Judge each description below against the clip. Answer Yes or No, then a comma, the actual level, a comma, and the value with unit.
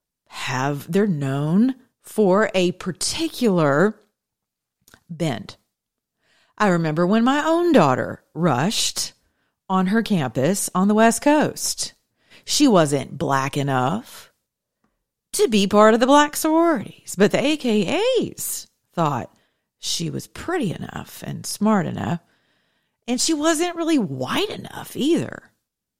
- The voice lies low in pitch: No, high, 210 Hz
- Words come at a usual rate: No, slow, 115 wpm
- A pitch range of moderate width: No, wide, 7.9 semitones